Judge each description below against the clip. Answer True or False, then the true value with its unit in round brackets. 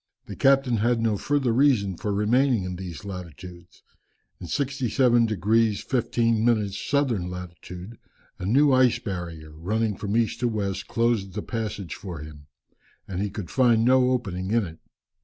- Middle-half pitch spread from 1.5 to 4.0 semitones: False (4.6 semitones)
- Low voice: True (110 Hz)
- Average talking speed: True (160 wpm)